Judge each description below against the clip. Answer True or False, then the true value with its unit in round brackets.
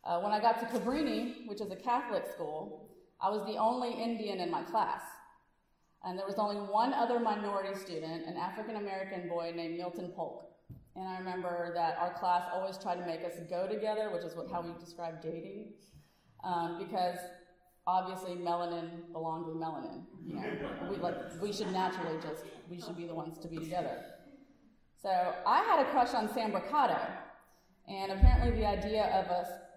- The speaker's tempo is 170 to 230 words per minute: True (180 wpm)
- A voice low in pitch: False (185 Hz)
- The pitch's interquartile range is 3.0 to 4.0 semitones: True (3.6 semitones)